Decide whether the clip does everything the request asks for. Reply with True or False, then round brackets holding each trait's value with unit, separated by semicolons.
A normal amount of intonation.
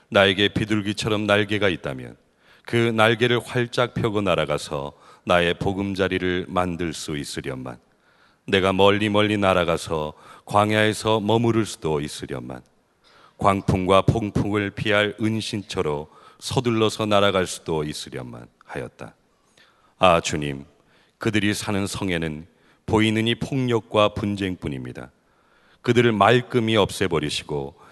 True (4.2 semitones)